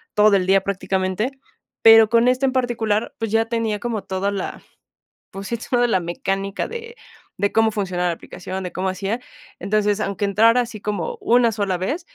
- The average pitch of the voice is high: Yes, high, 210 Hz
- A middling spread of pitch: Yes, average, 3.2 semitones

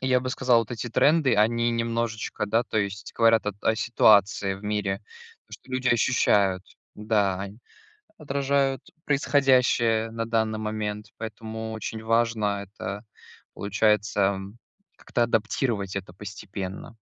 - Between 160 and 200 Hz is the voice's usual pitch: No, low, 110 Hz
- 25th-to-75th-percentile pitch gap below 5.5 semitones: Yes, narrow, 2.4 semitones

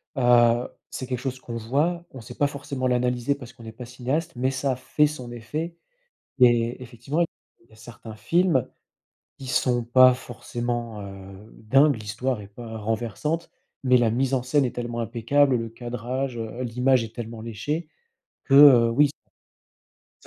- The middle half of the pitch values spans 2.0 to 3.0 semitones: Yes, narrow, 2.6 semitones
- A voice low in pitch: Yes, low, 125 Hz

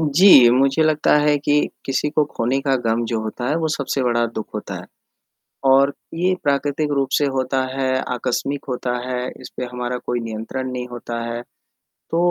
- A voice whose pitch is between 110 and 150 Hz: Yes, low, 135 Hz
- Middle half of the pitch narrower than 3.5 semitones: Yes, average, 3.0 semitones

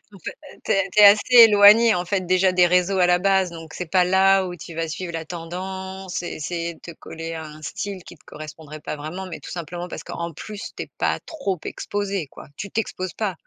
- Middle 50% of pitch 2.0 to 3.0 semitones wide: Yes, average, 2.7 semitones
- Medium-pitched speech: Yes, medium, 180 Hz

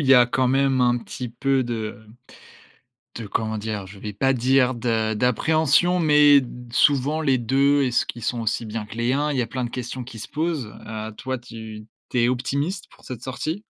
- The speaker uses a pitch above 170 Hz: No, low, 125 Hz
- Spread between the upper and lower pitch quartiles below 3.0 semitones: No, average, 3.4 semitones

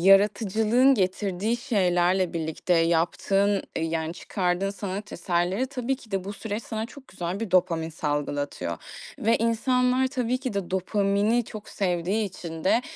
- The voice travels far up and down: No, average, 4.4 semitones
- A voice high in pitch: Yes, high, 195 Hz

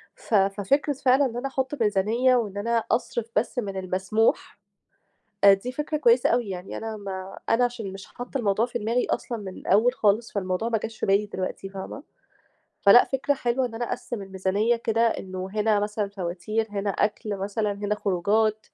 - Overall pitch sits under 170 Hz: No, high, 215 Hz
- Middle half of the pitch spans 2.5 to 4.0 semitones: Yes, average, 3.3 semitones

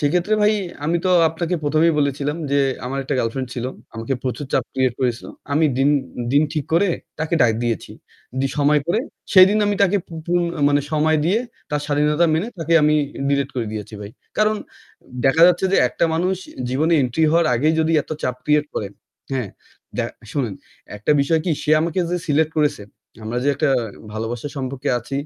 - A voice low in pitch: No, medium, 150 Hz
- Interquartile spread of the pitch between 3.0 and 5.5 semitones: Yes, average, 4.1 semitones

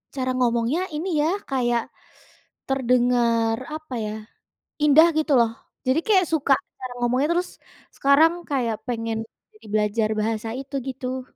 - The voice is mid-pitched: No, very high, 255 Hz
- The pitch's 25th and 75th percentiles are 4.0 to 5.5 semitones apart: No, average, 3.3 semitones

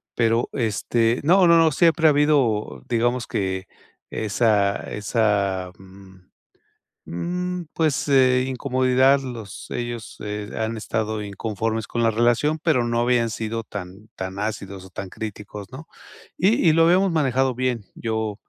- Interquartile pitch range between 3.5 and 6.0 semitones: Yes, average, 4.2 semitones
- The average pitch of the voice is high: No, low, 115 Hz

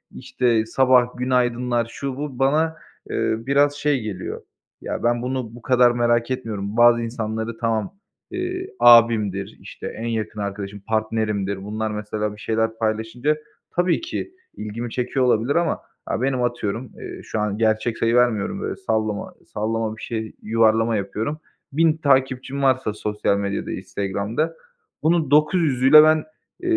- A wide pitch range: No, average, 3.4 semitones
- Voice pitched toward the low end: Yes, low, 115 Hz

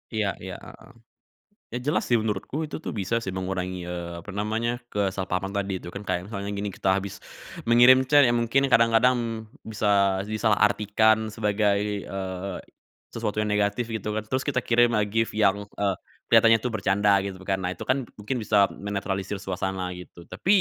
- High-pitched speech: No, low, 105 Hz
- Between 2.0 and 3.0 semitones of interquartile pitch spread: Yes, average, 2.7 semitones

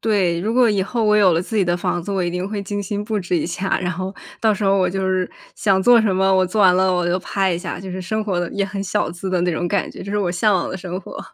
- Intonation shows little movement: Yes, narrow, 2.3 semitones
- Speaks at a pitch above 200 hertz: No, high, 190 Hz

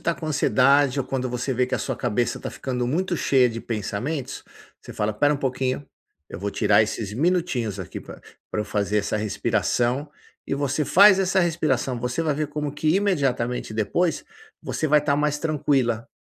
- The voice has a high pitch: No, low, 135 Hz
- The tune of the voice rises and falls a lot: No, average, 4.2 semitones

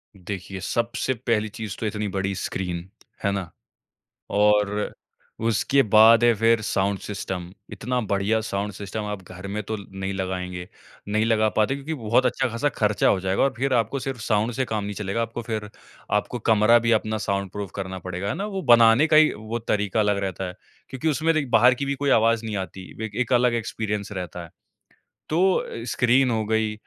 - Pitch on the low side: Yes, low, 110 Hz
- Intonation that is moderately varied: Yes, average, 3.0 semitones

